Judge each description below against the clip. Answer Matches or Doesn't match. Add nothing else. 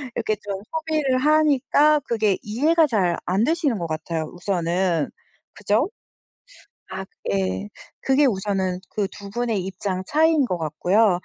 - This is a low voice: Doesn't match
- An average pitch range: Doesn't match